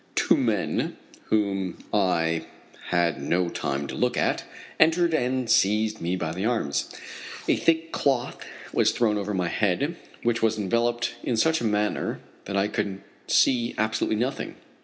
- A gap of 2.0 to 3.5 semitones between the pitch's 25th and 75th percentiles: No, average, 4.5 semitones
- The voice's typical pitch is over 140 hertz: No, low, 105 Hz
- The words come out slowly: No, average, 155 wpm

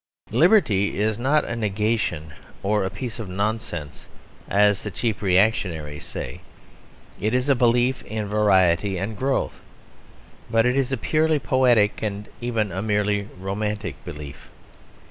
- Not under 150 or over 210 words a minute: No, average, 140 wpm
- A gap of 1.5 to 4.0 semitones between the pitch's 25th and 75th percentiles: Yes, average, 3.7 semitones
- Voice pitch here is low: Yes, low, 105 Hz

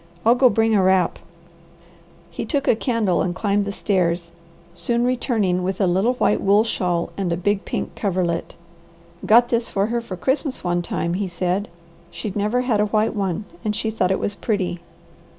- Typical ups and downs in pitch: Yes, average, 3.7 semitones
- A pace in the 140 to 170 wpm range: No, average, 185 wpm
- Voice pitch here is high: Yes, high, 200 Hz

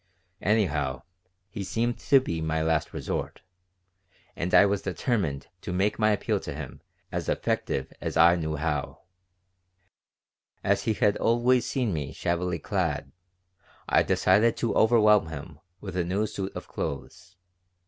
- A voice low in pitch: Yes, very low, 95 Hz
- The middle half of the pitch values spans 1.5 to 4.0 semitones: No, average, 5.2 semitones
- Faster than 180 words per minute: No, average, 145 wpm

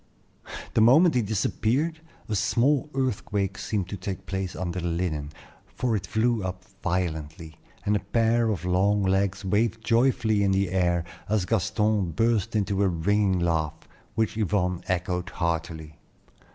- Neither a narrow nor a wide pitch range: Yes, average, 3.6 semitones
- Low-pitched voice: Yes, low, 100 Hz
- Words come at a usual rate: Yes, average, 150 wpm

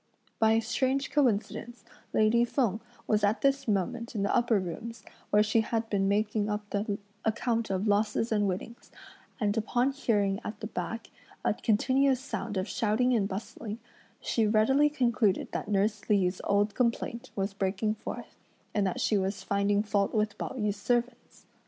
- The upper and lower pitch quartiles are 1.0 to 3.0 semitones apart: Yes, narrow, 2.5 semitones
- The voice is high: Yes, high, 215 Hz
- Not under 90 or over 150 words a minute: No, average, 165 wpm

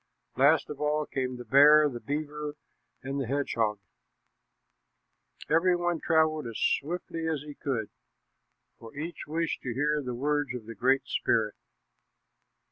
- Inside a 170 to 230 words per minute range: No, average, 140 wpm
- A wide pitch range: No, average, 3.3 semitones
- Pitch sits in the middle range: Yes, medium, 145 Hz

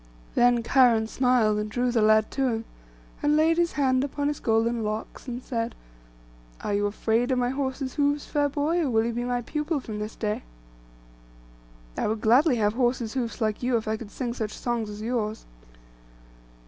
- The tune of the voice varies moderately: Yes, average, 3.2 semitones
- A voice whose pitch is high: Yes, high, 240 Hz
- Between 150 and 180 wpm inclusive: No, average, 190 wpm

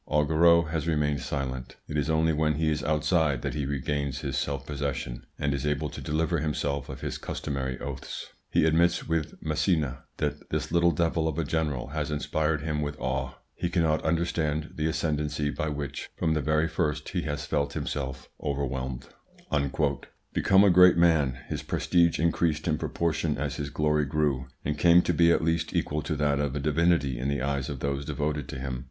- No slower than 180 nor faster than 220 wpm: Yes, average, 190 wpm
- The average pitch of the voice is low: Yes, very low, 75 Hz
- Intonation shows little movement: Yes, narrow, 2.3 semitones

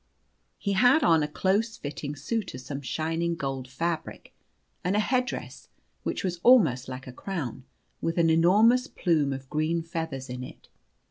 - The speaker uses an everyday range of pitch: No, wide, 6.3 semitones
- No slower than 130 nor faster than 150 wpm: No, average, 160 wpm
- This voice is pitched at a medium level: Yes, medium, 165 Hz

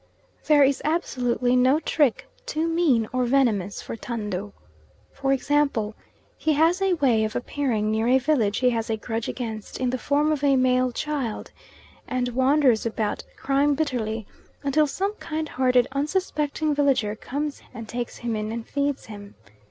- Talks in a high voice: Yes, very high, 255 Hz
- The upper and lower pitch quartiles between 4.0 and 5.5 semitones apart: Yes, average, 4.4 semitones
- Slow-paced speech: No, average, 160 wpm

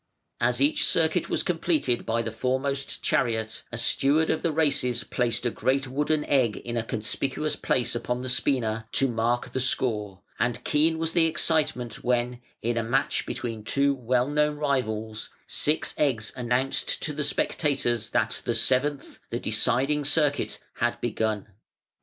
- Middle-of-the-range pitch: No, low, 125 Hz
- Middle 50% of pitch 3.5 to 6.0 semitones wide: Yes, average, 3.9 semitones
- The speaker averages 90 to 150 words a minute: No, average, 160 wpm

